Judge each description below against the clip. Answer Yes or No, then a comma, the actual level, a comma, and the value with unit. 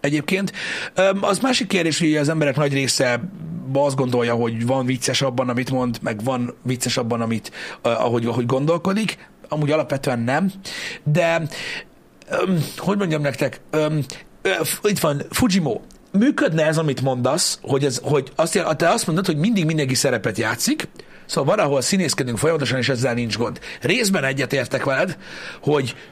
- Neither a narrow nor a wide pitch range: Yes, average, 4.9 semitones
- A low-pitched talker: No, medium, 150 Hz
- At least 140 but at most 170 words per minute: Yes, average, 145 wpm